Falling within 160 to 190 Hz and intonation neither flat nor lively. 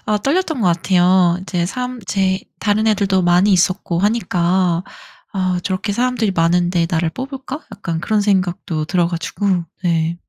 Yes: medium, 185 Hz; average, 3.2 semitones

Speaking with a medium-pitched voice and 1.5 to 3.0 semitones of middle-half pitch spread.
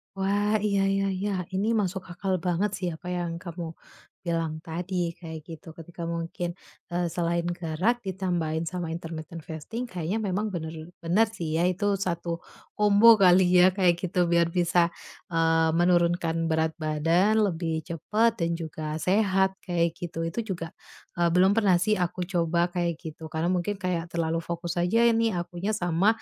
Yes: medium, 175 Hz; narrow, 2.5 semitones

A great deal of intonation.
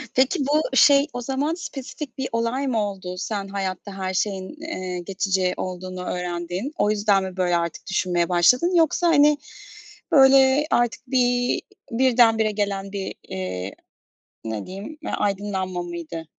Yes: wide, 6.3 semitones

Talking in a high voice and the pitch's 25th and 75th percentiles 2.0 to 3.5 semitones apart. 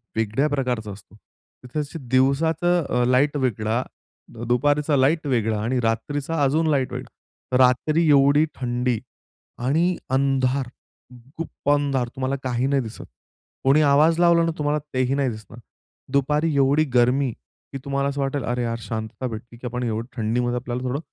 No: low, 130 Hz; average, 3.1 semitones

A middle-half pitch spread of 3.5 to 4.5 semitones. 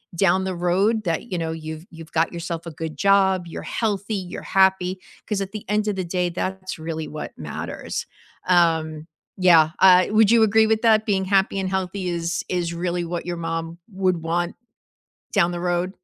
No: narrow, 2.5 semitones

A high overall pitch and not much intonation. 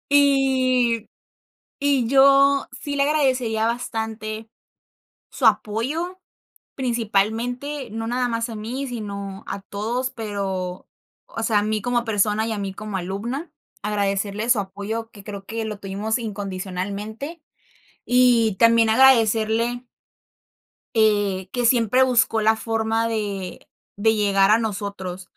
No: high, 225 Hz; average, 3.2 semitones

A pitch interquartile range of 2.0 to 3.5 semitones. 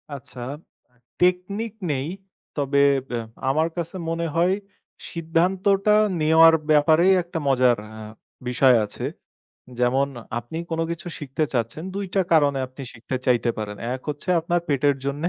No: average, 4.6 semitones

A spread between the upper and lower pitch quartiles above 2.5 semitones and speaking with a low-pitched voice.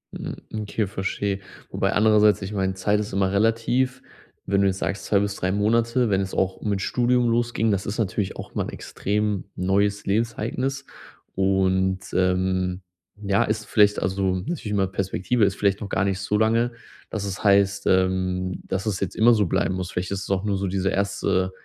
No: narrow, 2.1 semitones; low, 100 Hz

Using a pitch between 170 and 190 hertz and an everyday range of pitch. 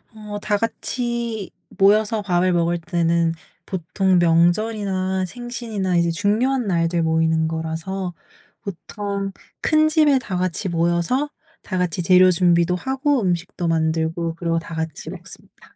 Yes: medium, 185 Hz; average, 4.0 semitones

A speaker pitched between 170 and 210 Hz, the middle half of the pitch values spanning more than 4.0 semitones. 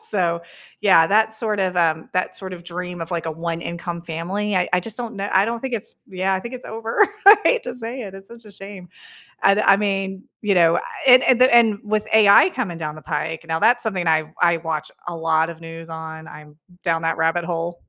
Yes: medium, 185 Hz; average, 4.4 semitones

